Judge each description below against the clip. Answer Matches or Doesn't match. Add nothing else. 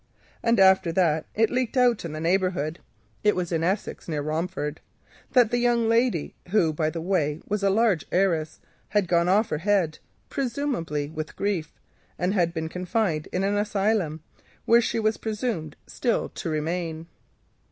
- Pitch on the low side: Doesn't match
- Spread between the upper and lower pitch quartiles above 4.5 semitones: Matches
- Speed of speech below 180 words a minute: Matches